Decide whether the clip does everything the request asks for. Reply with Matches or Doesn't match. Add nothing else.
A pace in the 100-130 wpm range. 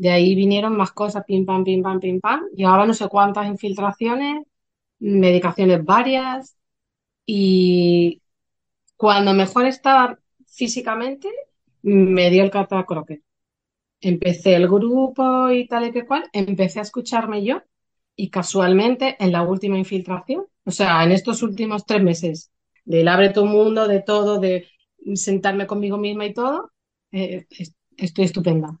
Doesn't match